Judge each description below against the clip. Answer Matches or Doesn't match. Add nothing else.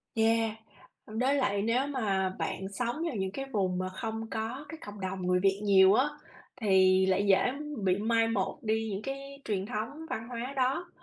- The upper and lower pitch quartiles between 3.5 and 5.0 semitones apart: Matches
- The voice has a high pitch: Matches